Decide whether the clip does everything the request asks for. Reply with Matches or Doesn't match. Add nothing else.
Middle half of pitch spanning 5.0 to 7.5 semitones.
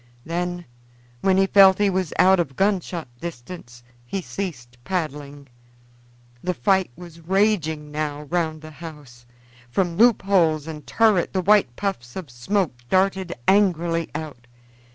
Doesn't match